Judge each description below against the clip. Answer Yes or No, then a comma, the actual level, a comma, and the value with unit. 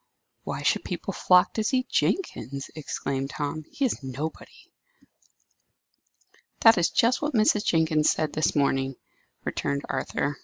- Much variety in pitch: Yes, wide, 7.4 semitones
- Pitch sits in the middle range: Yes, medium, 155 Hz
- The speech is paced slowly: Yes, slow, 130 wpm